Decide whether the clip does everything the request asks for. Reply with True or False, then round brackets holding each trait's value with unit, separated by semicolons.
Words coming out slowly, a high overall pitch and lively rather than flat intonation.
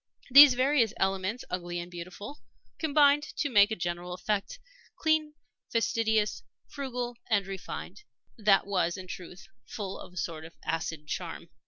False (145 wpm; 200 Hz; 5.7 semitones)